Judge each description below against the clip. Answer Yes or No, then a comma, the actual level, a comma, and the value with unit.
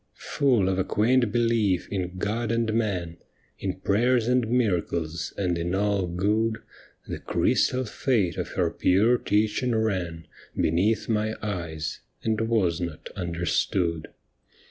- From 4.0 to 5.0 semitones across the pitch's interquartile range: Yes, average, 4.3 semitones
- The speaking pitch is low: Yes, low, 100 Hz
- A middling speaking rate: No, slow, 130 wpm